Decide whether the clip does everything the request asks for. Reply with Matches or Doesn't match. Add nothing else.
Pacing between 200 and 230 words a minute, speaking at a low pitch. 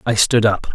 Doesn't match